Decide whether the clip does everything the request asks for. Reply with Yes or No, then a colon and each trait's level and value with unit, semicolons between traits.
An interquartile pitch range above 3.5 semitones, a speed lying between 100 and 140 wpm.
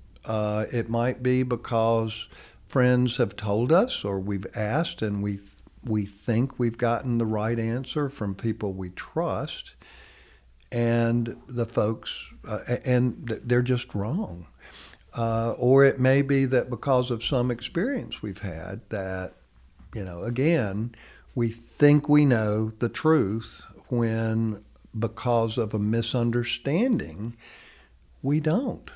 No: average, 2.9 semitones; slow, 135 wpm